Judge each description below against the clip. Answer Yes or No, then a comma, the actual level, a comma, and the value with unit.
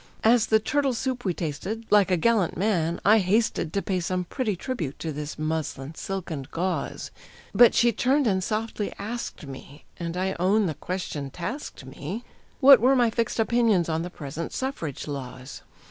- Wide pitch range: Yes, wide, 6.1 semitones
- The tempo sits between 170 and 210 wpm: Yes, average, 175 wpm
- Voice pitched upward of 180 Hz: Yes, high, 190 Hz